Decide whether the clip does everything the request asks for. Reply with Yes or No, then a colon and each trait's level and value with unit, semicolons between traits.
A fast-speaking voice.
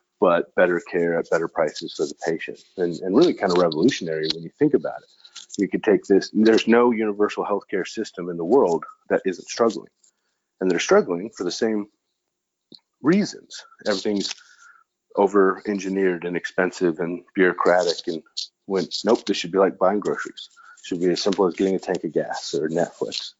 No: average, 180 wpm